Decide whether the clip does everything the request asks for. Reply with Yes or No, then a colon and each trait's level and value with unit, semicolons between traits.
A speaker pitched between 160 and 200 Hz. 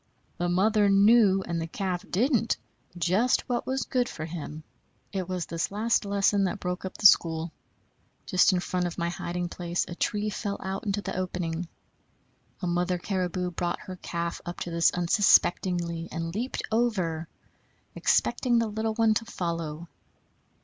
Yes: medium, 185 Hz